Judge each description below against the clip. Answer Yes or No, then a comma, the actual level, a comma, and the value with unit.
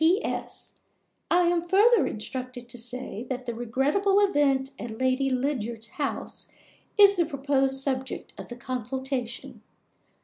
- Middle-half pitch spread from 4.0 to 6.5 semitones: Yes, average, 4.5 semitones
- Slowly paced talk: Yes, slow, 130 wpm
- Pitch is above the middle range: Yes, very high, 265 Hz